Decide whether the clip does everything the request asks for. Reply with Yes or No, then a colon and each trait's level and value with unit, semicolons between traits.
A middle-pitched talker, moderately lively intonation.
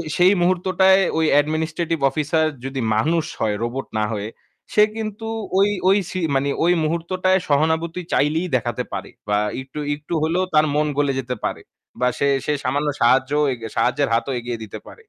Yes: medium, 155 Hz; average, 4.8 semitones